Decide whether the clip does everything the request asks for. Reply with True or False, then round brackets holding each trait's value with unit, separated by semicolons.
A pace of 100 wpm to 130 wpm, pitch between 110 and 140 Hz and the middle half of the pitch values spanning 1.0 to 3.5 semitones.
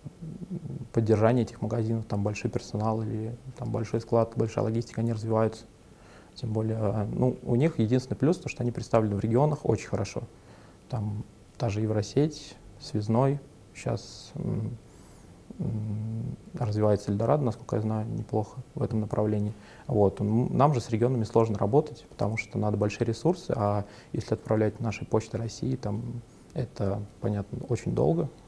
False (145 wpm; 115 Hz; 2.6 semitones)